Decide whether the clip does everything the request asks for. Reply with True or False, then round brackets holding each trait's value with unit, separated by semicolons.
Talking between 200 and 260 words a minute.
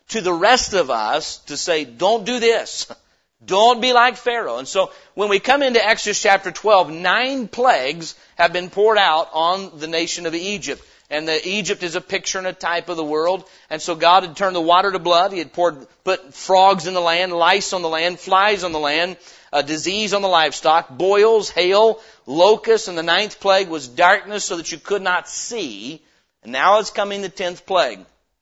True (205 wpm)